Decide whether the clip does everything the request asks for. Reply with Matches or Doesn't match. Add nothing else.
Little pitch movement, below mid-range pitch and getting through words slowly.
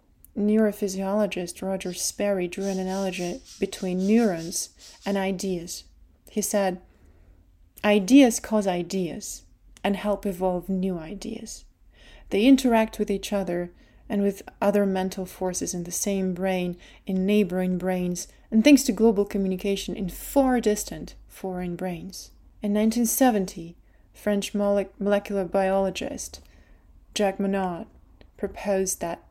Doesn't match